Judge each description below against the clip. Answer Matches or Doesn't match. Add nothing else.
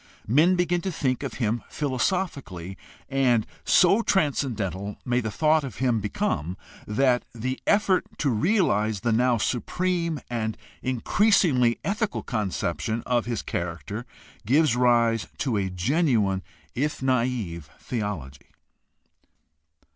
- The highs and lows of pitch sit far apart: Matches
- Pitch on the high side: Doesn't match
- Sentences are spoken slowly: Matches